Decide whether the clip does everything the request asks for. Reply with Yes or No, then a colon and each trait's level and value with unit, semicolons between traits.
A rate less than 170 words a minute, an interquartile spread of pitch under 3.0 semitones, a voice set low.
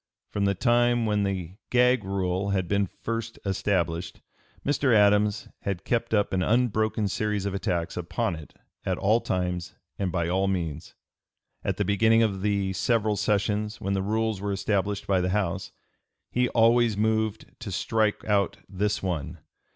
Yes: average, 160 wpm; narrow, 2.6 semitones; low, 100 Hz